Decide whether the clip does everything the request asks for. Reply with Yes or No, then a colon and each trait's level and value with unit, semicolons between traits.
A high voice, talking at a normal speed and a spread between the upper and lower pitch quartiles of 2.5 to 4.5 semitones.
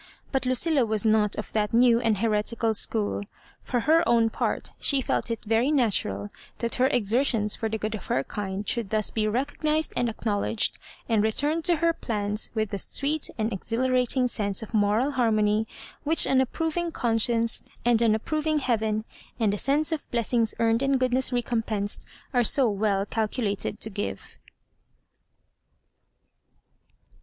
Yes: high, 230 Hz; average, 160 wpm; average, 3.4 semitones